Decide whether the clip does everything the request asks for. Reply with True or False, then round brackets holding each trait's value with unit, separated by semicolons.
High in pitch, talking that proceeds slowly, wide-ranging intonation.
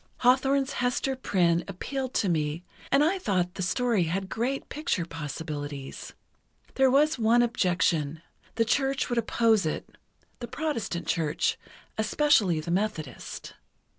True (215 Hz; 125 wpm; 7.5 semitones)